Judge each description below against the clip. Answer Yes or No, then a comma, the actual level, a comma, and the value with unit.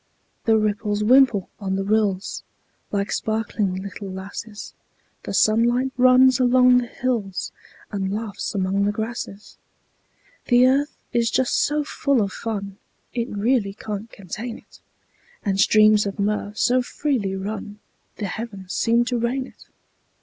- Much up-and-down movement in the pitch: No, average, 3.4 semitones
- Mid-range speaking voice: No, high, 215 Hz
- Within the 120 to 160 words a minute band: Yes, average, 140 wpm